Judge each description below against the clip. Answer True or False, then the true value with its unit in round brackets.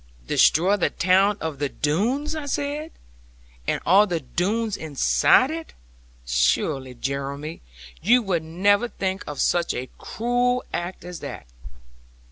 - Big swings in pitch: True (7.6 semitones)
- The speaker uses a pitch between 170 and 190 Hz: True (185 Hz)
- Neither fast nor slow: False (130 wpm)